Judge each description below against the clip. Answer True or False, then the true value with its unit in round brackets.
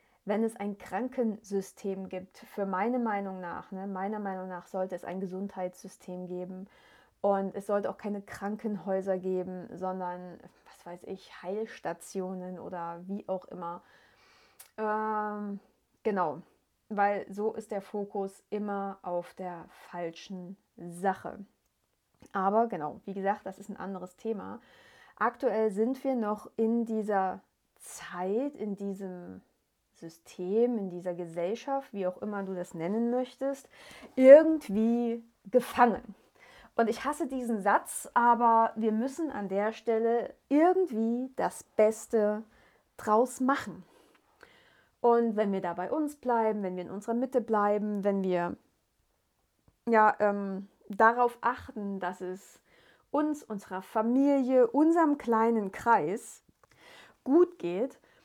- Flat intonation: False (3.7 semitones)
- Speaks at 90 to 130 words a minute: True (125 wpm)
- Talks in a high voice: True (205 Hz)